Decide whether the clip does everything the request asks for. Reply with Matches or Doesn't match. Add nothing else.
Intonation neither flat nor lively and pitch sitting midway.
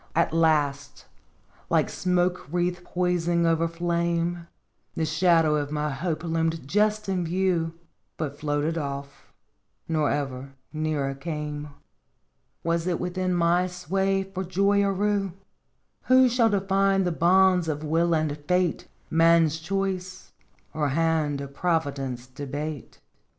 Matches